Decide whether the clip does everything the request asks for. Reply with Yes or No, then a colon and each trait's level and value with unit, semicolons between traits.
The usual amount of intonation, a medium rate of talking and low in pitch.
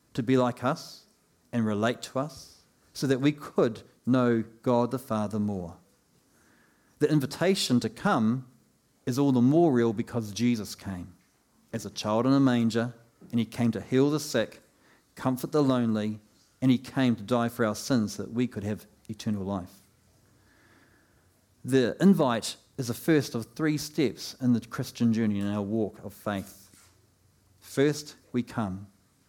Yes: average, 4.0 semitones; average, 165 wpm; low, 115 Hz